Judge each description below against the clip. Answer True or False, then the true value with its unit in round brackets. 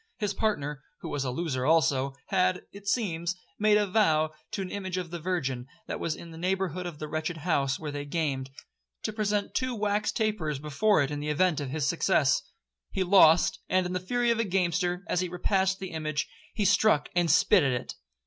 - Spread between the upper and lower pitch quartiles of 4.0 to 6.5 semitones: True (4.5 semitones)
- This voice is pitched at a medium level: True (175 Hz)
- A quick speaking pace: True (210 wpm)